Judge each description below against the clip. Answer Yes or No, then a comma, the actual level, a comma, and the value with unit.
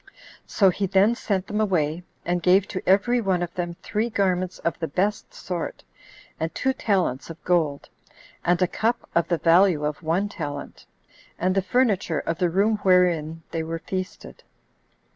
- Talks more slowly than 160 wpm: No, average, 170 wpm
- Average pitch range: Yes, average, 3.1 semitones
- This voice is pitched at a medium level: Yes, medium, 180 Hz